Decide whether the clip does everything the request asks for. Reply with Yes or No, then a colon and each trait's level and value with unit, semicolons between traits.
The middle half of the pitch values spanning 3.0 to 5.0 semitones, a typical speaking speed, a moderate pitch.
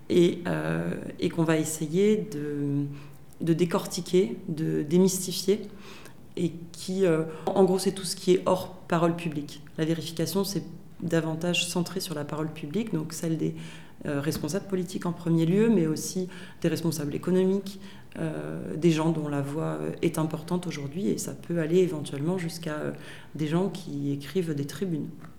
Yes: average, 3.3 semitones; average, 165 wpm; medium, 165 Hz